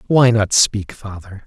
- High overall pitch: No, low, 105 Hz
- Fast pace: No, average, 165 wpm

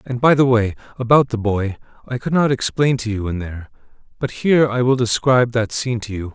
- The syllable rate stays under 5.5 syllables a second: No, 6.0 syllables/s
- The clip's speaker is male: Yes, male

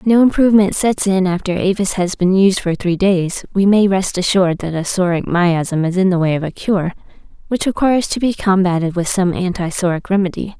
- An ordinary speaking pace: No, fast, 215 wpm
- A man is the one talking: No, female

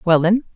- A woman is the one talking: Yes, female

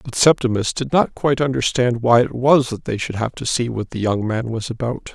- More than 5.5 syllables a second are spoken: No, 5.4 syllables/s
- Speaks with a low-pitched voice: Yes, low, 120 Hz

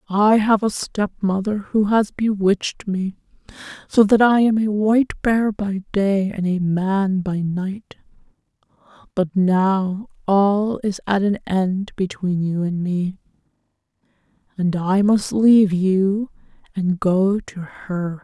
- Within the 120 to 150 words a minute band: Yes, average, 140 wpm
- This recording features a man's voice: No, female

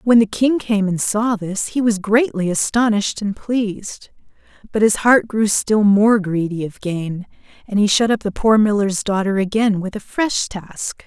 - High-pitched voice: Yes, high, 210 Hz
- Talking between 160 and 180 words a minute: No, average, 190 wpm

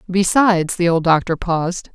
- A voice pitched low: No, medium, 180 Hz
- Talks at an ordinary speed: Yes, average, 155 wpm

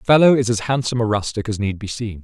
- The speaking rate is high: Yes, fast, 295 wpm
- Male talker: Yes, male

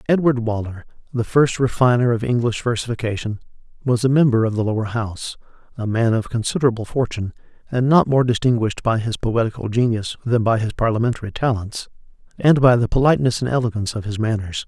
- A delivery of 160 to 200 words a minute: Yes, average, 170 wpm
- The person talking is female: No, male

